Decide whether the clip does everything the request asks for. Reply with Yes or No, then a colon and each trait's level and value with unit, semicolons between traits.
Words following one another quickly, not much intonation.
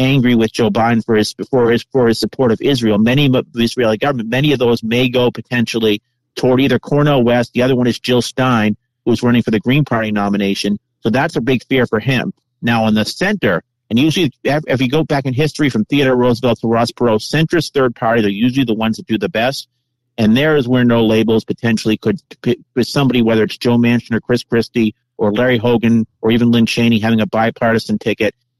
Yes: fast, 220 wpm; narrow, 2.3 semitones